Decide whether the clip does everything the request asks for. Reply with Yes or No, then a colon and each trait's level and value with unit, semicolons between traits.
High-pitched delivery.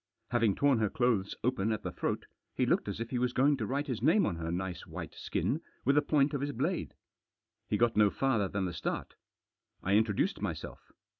No: low, 115 Hz